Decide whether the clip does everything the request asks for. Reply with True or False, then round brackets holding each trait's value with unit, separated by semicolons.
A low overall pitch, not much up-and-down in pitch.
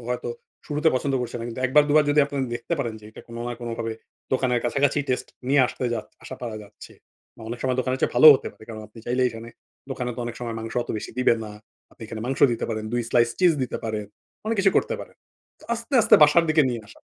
False (125 Hz; 3.7 semitones)